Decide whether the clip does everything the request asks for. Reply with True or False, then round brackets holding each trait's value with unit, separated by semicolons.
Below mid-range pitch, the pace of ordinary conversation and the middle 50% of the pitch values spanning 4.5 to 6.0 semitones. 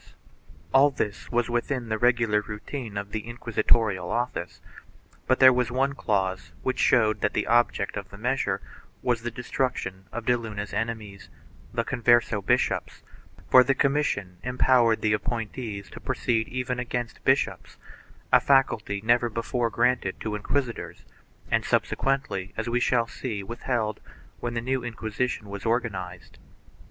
False (115 Hz; 150 wpm; 3.0 semitones)